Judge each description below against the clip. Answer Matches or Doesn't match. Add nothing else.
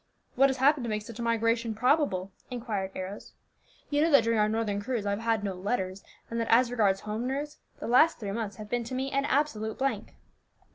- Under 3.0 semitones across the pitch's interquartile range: Doesn't match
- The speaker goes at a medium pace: Doesn't match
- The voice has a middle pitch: Doesn't match